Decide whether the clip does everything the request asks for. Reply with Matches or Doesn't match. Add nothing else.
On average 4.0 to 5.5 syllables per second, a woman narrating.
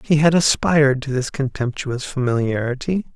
Doesn't match